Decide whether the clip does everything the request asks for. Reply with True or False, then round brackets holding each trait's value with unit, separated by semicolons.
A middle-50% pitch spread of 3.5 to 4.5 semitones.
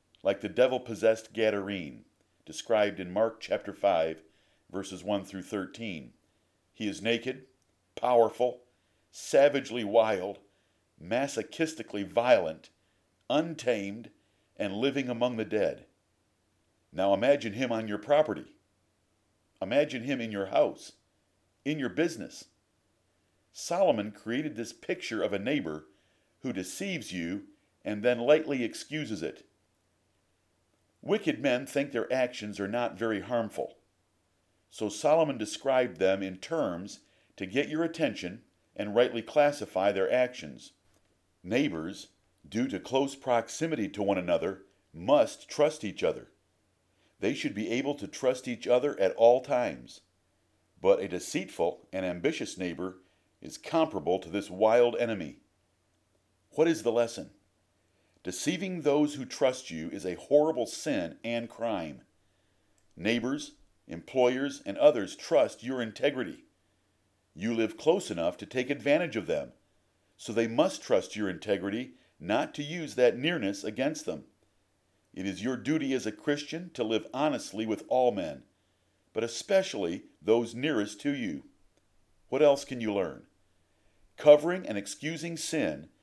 False (5.5 semitones)